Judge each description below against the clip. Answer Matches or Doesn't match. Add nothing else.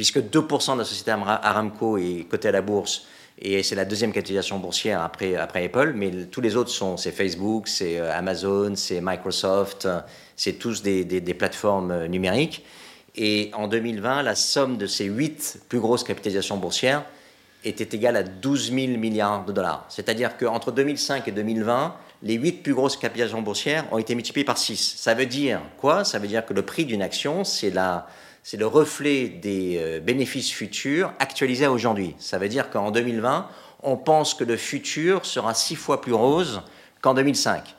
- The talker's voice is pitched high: Doesn't match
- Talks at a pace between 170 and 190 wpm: Matches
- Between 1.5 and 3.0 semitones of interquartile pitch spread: Doesn't match